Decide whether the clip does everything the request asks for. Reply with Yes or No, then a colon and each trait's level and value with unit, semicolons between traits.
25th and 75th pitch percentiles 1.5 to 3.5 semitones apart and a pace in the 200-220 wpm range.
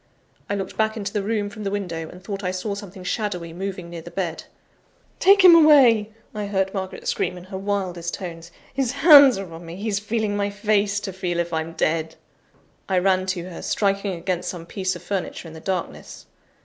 Yes: average, 2.8 semitones; fast, 205 wpm